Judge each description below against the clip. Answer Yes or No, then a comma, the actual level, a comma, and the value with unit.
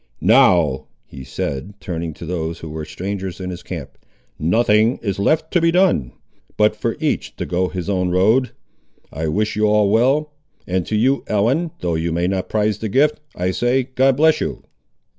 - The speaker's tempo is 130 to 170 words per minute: No, average, 185 wpm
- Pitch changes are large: Yes, wide, 6.2 semitones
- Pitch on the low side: Yes, low, 100 Hz